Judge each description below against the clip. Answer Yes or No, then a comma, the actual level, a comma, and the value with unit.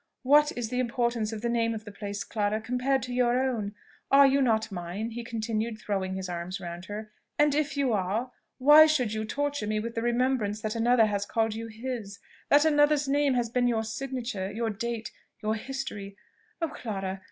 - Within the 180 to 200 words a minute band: Yes, average, 195 wpm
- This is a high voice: Yes, high, 230 Hz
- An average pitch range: Yes, average, 3.4 semitones